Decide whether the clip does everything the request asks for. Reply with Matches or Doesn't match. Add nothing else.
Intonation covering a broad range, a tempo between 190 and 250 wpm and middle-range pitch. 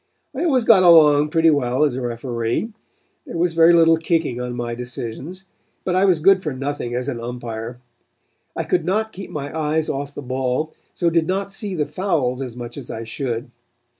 Matches